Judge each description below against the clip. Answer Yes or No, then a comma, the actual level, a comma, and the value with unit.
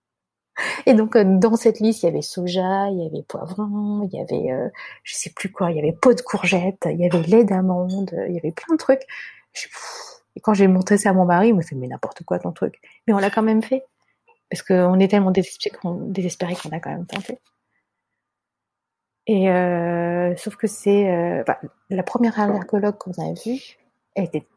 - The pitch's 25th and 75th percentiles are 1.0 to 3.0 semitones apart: No, average, 3.8 semitones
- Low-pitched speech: No, high, 195 Hz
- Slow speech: No, average, 210 wpm